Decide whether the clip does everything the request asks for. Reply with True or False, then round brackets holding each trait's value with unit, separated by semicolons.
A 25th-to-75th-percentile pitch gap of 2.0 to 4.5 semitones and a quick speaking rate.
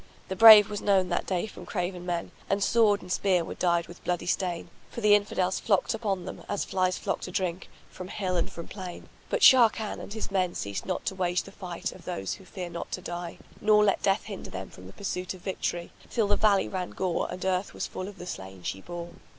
True (2.5 semitones; 240 wpm)